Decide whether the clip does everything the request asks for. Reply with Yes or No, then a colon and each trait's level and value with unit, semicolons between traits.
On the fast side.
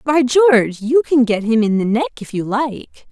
Yes: fast, 230 wpm